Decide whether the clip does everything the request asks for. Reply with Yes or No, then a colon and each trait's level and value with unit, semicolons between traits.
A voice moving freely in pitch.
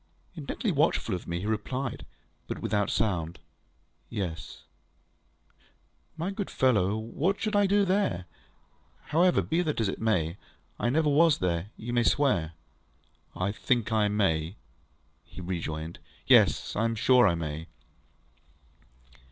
Yes: wide, 8.6 semitones